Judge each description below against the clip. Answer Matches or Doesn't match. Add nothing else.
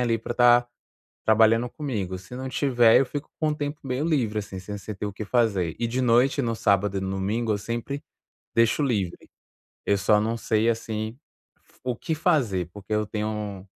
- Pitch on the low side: Matches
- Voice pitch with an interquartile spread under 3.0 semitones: Doesn't match